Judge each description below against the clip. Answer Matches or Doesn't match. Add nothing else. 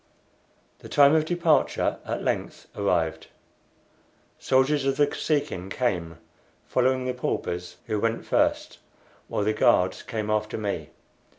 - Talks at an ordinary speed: Doesn't match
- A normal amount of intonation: Doesn't match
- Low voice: Matches